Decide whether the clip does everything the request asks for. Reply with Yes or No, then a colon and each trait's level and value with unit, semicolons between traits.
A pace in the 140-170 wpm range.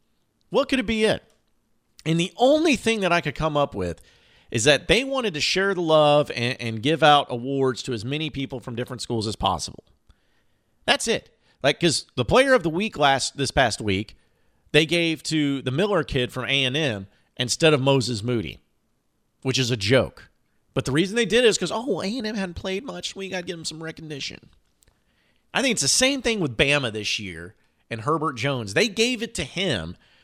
No: fast, 205 wpm